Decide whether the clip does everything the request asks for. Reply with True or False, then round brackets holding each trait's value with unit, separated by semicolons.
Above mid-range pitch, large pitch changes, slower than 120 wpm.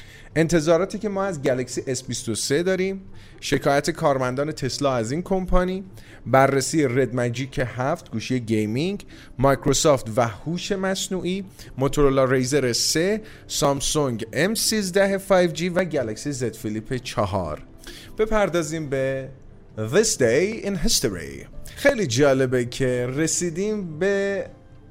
False (140 Hz; 6.6 semitones; 110 wpm)